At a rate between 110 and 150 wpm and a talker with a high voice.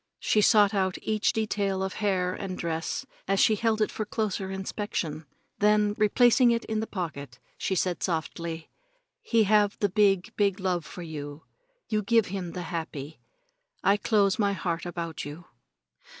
No: average, 165 wpm; high, 195 Hz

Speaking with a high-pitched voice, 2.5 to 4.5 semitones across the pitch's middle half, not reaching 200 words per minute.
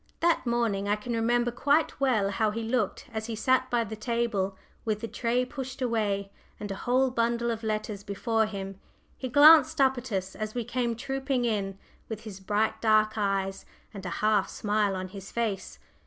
Yes: high, 220 Hz; average, 3.0 semitones; average, 190 wpm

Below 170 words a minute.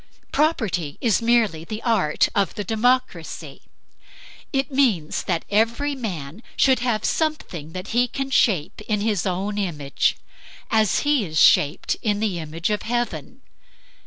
Yes: average, 140 wpm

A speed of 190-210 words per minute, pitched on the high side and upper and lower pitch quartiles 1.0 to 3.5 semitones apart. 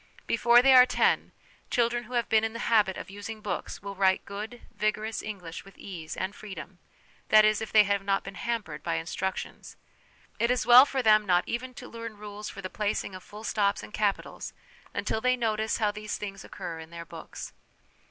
Yes: average, 200 wpm; high, 210 Hz; average, 2.7 semitones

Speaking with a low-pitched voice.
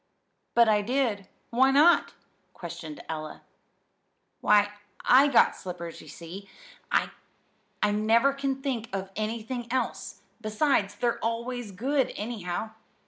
No: high, 225 Hz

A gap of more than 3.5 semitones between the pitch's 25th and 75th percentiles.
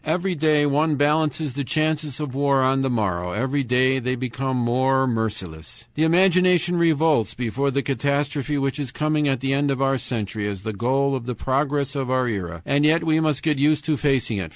No: average, 3.2 semitones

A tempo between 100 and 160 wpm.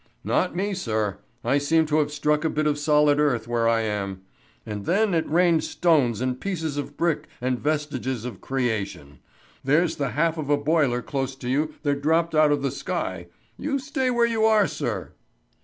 No: average, 190 wpm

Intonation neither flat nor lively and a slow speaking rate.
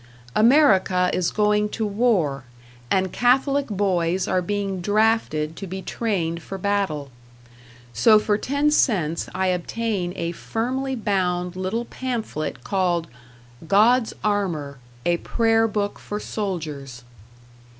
Yes: average, 4.3 semitones; slow, 120 wpm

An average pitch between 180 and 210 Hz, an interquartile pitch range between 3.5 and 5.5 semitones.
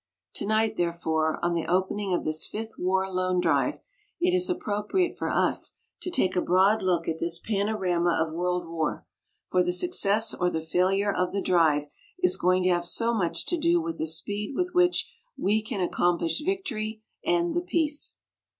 Yes: high, 190 Hz; average, 4.6 semitones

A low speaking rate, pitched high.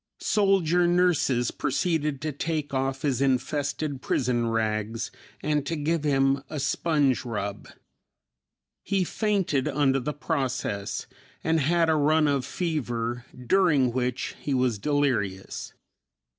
No: slow, 120 wpm; medium, 140 Hz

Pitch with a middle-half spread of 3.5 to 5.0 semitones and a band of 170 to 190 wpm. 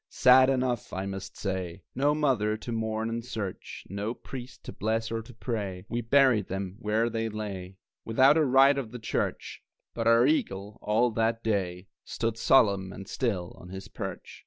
Yes: average, 3.8 semitones; average, 180 wpm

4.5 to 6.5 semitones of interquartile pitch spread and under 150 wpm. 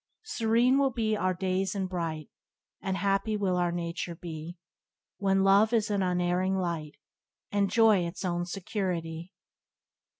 No: average, 2.8 semitones; average, 140 wpm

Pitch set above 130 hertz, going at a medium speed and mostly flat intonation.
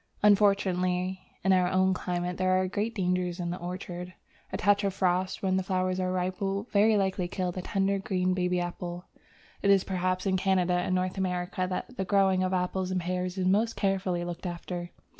Yes: medium, 185 Hz; average, 195 wpm; narrow, 1.2 semitones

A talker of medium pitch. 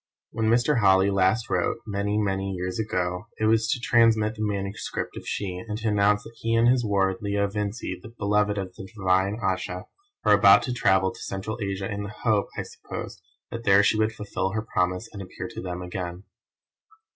No: low, 100 Hz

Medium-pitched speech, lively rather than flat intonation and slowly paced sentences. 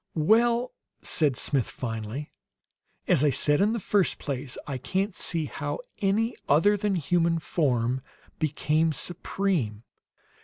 Yes: medium, 155 Hz; wide, 6.2 semitones; slow, 130 wpm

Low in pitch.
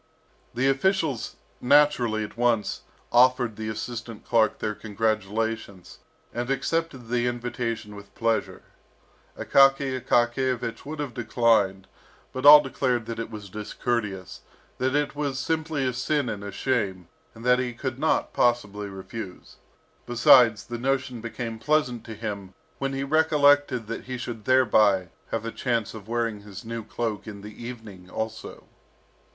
Yes: low, 120 Hz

